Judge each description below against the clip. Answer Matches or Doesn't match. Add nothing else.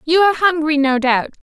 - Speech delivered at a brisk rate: Doesn't match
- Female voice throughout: Matches